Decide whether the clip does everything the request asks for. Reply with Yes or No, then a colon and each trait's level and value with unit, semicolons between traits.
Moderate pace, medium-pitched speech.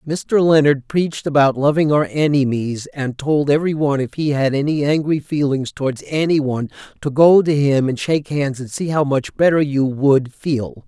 Yes: average, 190 wpm; medium, 145 Hz